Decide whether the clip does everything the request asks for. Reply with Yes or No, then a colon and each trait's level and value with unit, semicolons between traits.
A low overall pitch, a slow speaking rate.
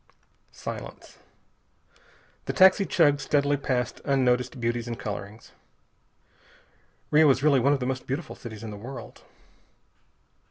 Yes: low, 130 Hz; slow, 125 wpm